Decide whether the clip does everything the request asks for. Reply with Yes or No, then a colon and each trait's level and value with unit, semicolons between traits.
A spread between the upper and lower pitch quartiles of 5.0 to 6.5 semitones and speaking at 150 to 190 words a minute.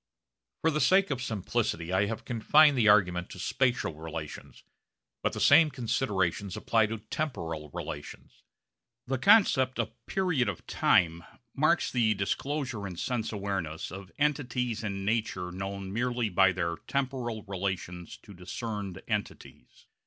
No: wide, 5.4 semitones; average, 140 wpm